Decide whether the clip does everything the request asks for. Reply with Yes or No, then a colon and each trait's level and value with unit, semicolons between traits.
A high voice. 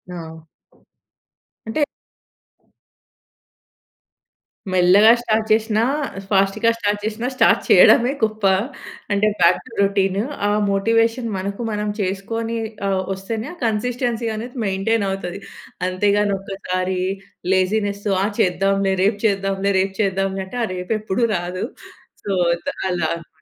Yes: high, 200 Hz